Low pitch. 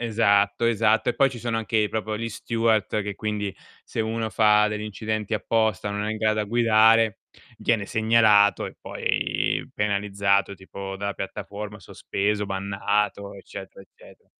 Yes: low, 105 Hz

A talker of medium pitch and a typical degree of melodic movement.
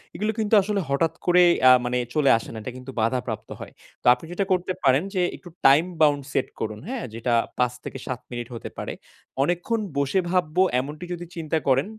No: medium, 150 Hz; wide, 5.9 semitones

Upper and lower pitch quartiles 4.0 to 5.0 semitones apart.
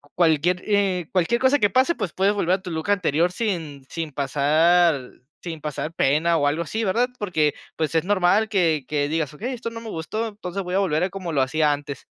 Yes: average, 4.6 semitones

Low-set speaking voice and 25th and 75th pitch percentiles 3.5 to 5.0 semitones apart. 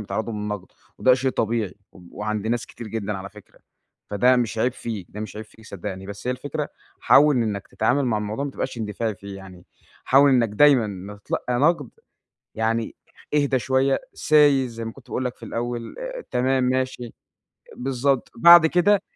Yes: low, 120 Hz; average, 4.0 semitones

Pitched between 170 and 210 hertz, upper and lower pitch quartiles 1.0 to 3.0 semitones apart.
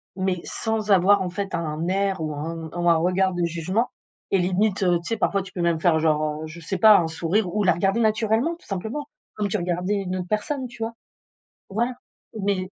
No: medium, 185 Hz; average, 3.6 semitones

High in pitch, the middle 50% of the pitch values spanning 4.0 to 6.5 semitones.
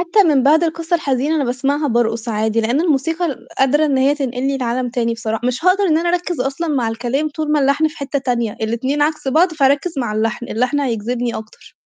Yes: very high, 270 Hz; average, 4.4 semitones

